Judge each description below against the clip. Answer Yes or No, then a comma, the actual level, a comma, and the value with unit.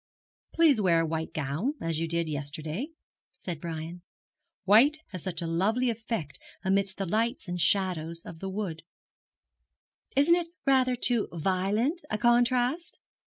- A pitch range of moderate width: No, wide, 6.5 semitones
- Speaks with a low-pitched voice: No, high, 195 Hz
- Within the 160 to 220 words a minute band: No, average, 145 wpm